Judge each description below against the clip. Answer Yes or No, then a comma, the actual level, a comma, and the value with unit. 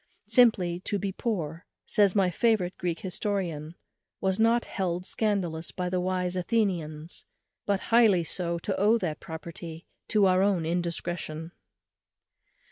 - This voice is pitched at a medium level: Yes, medium, 180 Hz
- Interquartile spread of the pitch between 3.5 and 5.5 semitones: No, average, 3.0 semitones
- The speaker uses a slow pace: Yes, slow, 130 wpm